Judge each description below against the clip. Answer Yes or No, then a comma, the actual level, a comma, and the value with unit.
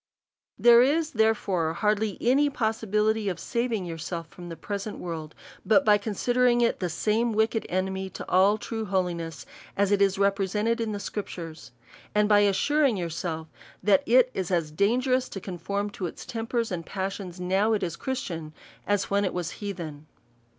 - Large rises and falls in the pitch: No, average, 3.8 semitones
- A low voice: No, high, 200 Hz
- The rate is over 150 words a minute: Yes, average, 175 wpm